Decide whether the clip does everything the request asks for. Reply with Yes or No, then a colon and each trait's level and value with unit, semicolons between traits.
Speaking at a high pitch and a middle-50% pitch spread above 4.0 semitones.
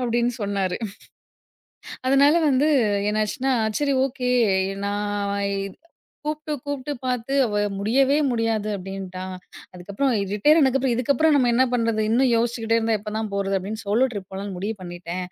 Yes: high, 230 Hz; average, 4.7 semitones